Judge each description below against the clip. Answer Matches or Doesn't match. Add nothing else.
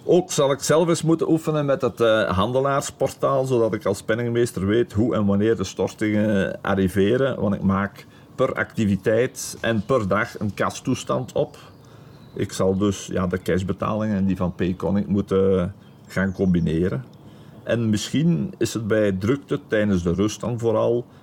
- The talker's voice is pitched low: Matches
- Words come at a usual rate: Matches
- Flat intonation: Doesn't match